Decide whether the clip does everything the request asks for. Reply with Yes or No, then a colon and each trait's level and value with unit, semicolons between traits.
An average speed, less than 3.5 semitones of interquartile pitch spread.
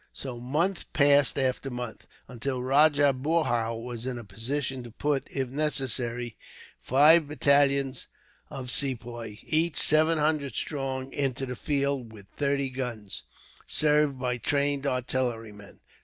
No: slow, 125 wpm; average, 2.8 semitones